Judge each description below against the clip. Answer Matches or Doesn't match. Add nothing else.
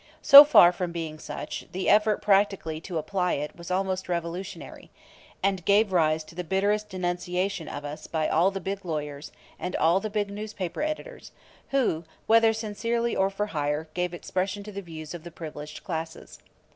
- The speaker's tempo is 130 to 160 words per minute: Doesn't match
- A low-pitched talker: Doesn't match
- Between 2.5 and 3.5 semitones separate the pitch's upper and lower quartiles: Doesn't match